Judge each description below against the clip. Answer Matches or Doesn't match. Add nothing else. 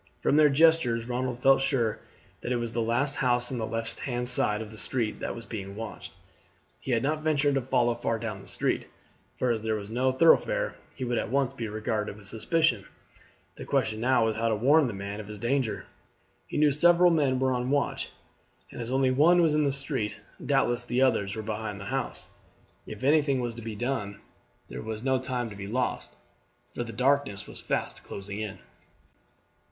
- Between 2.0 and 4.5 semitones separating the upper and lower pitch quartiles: Matches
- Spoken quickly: Matches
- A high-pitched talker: Doesn't match